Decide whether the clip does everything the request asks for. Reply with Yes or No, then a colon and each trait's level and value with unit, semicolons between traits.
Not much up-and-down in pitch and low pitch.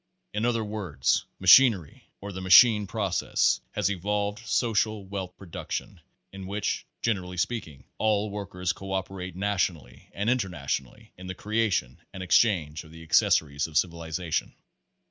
No: average, 3.5 semitones; very low, 95 Hz